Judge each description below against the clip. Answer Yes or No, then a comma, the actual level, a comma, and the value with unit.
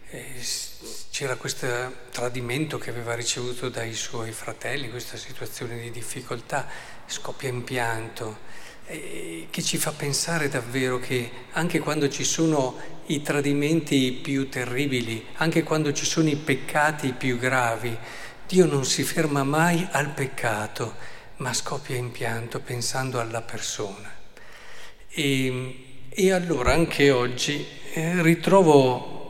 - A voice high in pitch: No, low, 130 Hz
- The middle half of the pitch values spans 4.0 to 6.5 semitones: No, average, 3.4 semitones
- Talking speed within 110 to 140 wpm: Yes, average, 120 wpm